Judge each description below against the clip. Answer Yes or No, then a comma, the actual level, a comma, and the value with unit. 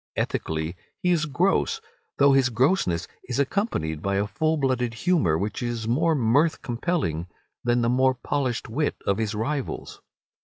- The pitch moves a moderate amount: No, wide, 5.8 semitones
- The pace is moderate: Yes, average, 155 wpm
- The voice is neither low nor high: No, low, 125 Hz